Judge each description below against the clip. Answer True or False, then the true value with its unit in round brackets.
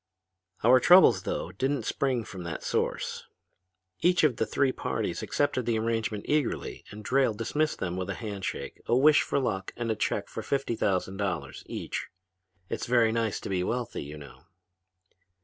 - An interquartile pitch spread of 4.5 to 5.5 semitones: True (5.1 semitones)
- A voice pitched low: True (115 Hz)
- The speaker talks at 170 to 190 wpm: True (175 wpm)